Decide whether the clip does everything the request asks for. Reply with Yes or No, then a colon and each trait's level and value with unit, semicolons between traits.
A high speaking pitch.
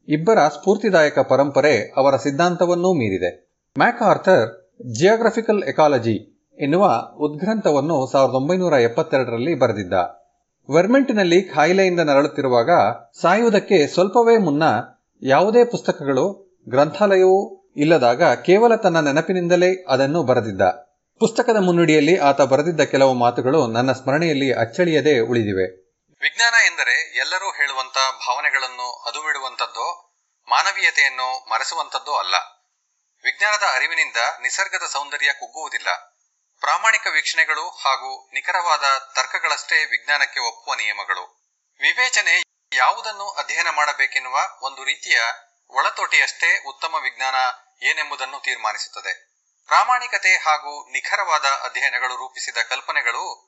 No: medium, 155 Hz